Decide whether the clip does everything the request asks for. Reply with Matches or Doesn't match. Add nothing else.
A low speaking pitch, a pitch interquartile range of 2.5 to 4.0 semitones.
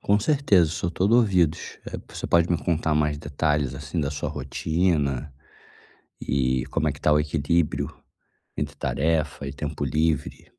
Matches